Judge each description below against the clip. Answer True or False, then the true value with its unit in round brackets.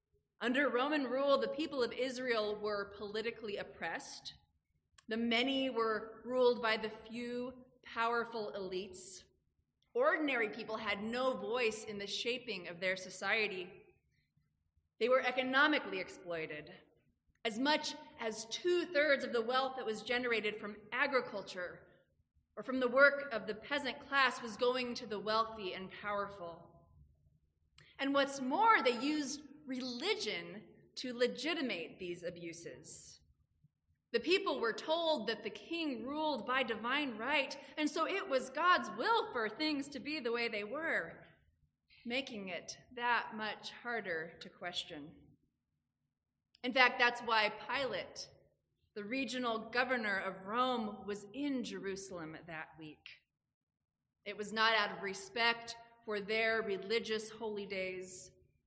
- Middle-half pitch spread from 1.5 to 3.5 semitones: False (4.3 semitones)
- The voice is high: True (230 Hz)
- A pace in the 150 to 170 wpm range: False (135 wpm)